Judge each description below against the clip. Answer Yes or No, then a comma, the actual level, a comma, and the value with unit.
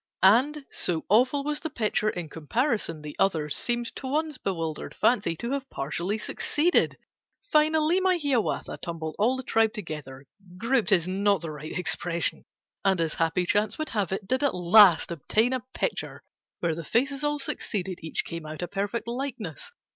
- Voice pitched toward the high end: Yes, high, 210 Hz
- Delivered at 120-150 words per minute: No, average, 170 wpm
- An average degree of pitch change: No, wide, 7.7 semitones